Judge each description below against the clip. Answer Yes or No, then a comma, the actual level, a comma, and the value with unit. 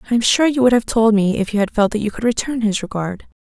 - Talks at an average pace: No, fast, 315 wpm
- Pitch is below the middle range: No, high, 220 Hz